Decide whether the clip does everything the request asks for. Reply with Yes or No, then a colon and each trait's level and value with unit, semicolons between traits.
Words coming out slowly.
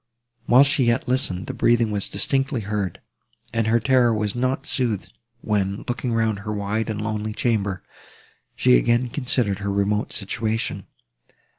No: average, 150 wpm